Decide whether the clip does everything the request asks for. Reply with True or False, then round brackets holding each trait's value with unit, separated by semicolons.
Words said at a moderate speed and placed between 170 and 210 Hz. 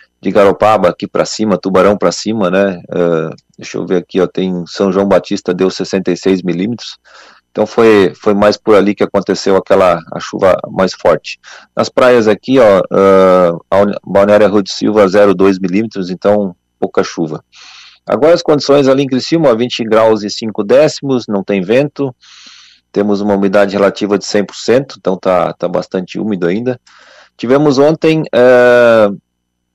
False (160 wpm; 100 Hz)